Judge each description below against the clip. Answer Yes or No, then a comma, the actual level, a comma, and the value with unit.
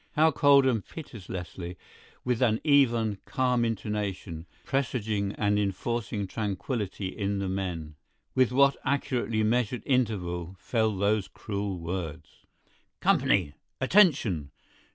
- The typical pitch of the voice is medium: No, low, 105 Hz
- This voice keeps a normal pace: No, slow, 105 wpm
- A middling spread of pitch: Yes, average, 4.7 semitones